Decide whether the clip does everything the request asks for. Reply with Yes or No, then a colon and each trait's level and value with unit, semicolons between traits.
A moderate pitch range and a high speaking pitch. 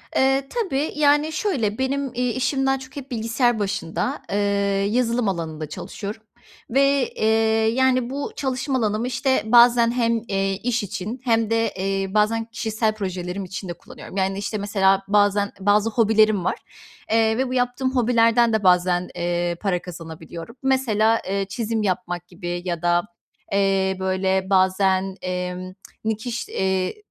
Yes: average, 4.5 semitones; high, 215 Hz